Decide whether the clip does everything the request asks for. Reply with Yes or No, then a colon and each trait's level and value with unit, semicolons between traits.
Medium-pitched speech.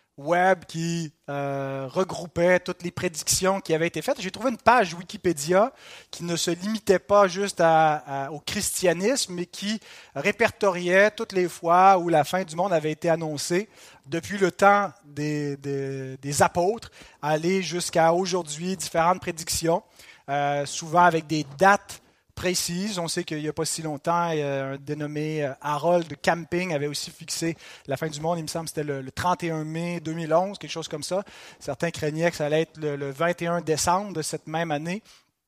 Yes: medium, 170 Hz